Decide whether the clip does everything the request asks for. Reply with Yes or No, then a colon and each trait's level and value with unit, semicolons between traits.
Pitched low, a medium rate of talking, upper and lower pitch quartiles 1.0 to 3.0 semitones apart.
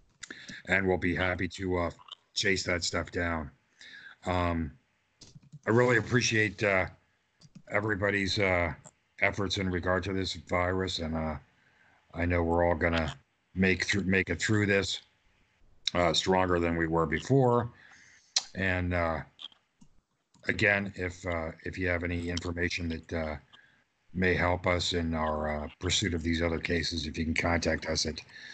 Yes: very low, 90 Hz; average, 150 wpm; narrow, 2.4 semitones